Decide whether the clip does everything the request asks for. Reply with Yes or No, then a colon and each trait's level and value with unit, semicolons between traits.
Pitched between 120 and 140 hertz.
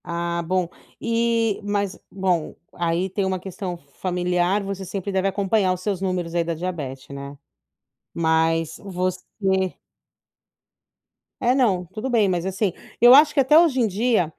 No: medium, 185 Hz